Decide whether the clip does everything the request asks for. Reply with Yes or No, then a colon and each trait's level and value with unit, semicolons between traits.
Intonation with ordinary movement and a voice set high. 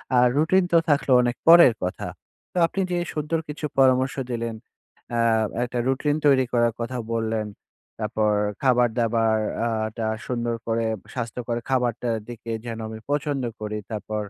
No: average, 3.0 semitones; low, 120 Hz